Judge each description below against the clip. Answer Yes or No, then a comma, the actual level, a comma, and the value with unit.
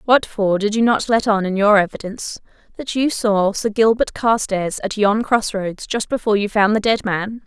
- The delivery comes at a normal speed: No, fast, 215 wpm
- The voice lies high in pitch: Yes, high, 210 Hz